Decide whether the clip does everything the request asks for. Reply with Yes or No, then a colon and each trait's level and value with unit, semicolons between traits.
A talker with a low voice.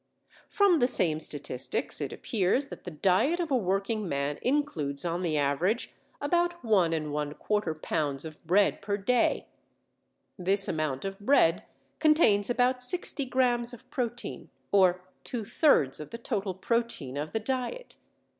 No: high, 200 Hz